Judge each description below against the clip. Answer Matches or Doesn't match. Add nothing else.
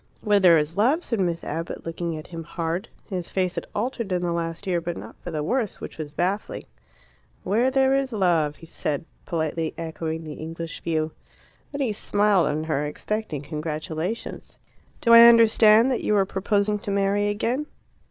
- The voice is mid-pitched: Matches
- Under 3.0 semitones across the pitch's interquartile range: Doesn't match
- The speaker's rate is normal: Matches